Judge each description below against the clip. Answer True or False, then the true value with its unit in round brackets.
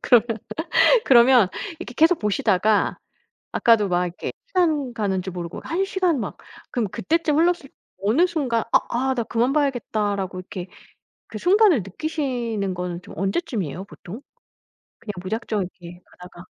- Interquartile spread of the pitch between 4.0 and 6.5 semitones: False (7.2 semitones)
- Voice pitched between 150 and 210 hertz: False (230 Hz)